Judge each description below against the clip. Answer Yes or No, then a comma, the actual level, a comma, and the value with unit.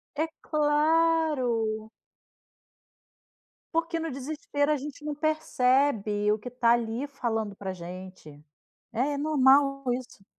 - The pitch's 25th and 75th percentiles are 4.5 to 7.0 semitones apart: Yes, average, 5.2 semitones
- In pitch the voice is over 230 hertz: Yes, very high, 265 Hz